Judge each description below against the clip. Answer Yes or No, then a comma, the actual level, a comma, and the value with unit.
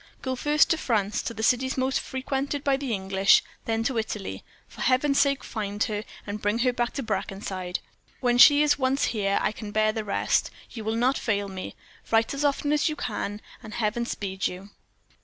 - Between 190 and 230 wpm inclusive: Yes, average, 200 wpm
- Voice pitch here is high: Yes, high, 225 Hz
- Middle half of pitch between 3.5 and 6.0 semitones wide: Yes, average, 4.4 semitones